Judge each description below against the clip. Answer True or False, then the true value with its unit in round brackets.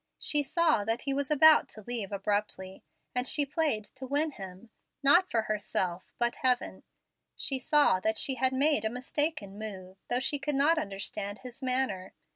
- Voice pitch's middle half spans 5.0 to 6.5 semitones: True (5.6 semitones)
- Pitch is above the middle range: True (250 Hz)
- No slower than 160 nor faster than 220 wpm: True (175 wpm)